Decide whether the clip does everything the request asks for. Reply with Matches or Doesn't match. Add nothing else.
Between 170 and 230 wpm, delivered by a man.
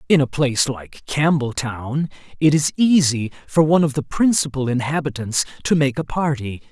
Doesn't match